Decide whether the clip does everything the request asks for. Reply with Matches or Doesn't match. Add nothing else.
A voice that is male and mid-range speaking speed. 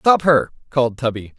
Matches